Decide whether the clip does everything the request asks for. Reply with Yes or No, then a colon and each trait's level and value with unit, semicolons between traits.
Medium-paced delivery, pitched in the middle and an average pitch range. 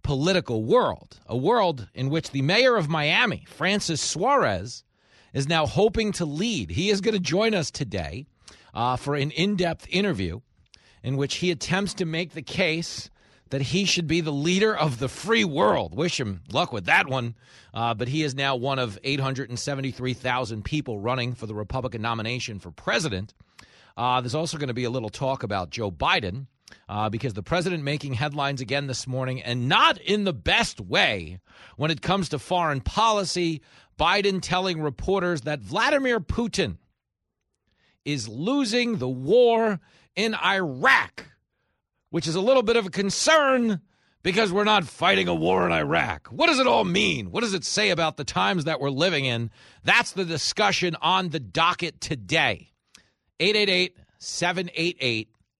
No: average, 170 wpm; medium, 150 Hz; wide, 6.9 semitones